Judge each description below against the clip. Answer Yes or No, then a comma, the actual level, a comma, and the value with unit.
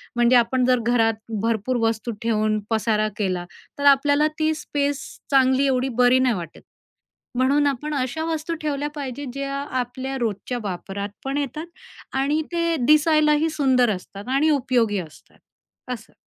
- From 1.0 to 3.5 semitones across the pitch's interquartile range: No, average, 4.0 semitones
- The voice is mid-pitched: No, very high, 260 Hz